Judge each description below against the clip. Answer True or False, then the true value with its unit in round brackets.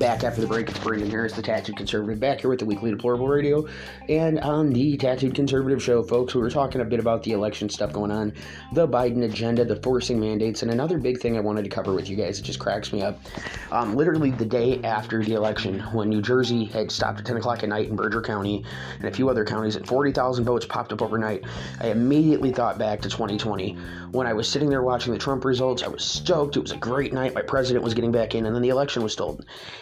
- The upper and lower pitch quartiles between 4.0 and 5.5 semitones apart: False (3.2 semitones)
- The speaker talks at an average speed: False (245 wpm)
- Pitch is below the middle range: True (115 Hz)